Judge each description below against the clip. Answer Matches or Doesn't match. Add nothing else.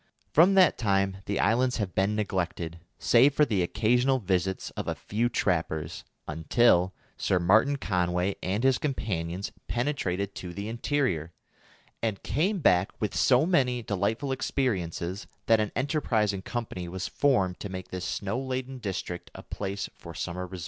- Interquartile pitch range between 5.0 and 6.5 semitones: Matches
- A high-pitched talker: Doesn't match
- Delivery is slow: Doesn't match